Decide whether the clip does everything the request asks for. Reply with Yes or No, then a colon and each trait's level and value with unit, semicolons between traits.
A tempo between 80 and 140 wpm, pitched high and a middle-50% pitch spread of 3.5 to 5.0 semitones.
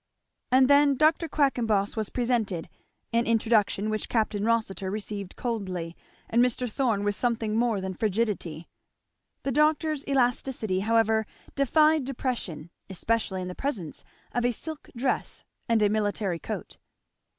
Yes: slow, 135 wpm; high, 225 Hz; average, 4.0 semitones